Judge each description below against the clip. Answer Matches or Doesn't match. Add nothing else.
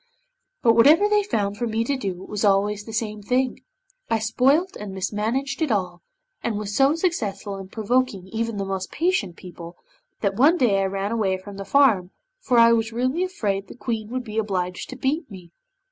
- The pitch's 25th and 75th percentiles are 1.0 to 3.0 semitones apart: Doesn't match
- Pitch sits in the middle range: Doesn't match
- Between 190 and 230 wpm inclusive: Matches